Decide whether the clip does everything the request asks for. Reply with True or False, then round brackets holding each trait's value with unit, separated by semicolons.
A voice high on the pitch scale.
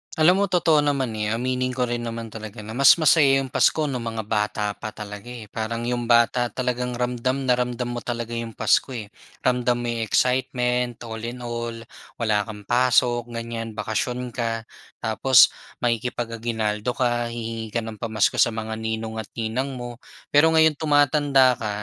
False (120 Hz)